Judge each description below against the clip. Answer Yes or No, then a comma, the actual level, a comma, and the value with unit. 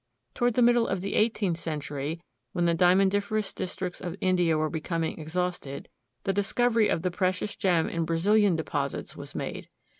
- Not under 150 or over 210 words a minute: Yes, average, 160 wpm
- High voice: No, medium, 180 Hz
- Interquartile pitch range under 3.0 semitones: No, average, 3.6 semitones